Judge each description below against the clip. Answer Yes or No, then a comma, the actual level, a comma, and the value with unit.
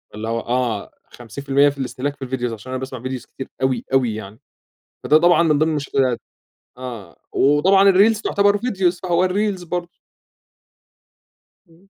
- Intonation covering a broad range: Yes, wide, 5.9 semitones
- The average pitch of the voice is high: No, medium, 140 Hz